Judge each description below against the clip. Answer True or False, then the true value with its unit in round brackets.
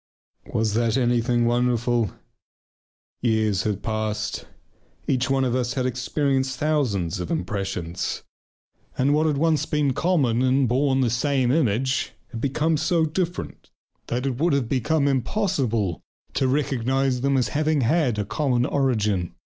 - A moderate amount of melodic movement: True (3.6 semitones)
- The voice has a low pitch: True (130 Hz)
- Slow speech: False (145 wpm)